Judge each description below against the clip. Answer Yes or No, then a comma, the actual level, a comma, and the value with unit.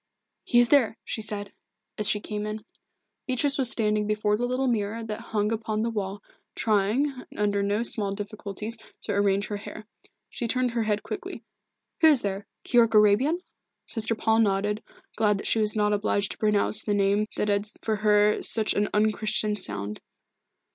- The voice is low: No, high, 210 Hz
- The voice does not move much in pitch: Yes, narrow, 1.7 semitones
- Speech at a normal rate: Yes, average, 175 wpm